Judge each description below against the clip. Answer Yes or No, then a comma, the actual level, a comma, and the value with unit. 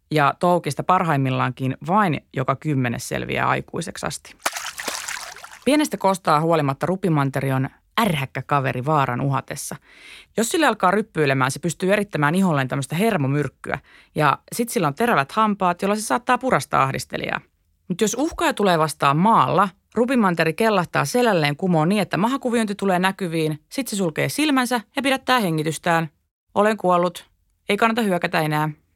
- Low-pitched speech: No, medium, 175 Hz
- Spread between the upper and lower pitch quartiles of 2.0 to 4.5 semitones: No, wide, 6.9 semitones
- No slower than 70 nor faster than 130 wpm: No, average, 140 wpm